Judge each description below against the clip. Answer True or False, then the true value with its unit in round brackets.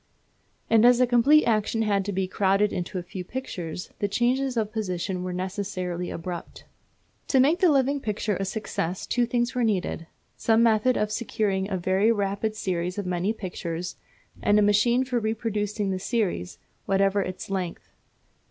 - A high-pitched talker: True (205 Hz)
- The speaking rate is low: False (170 wpm)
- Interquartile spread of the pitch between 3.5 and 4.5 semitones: True (3.8 semitones)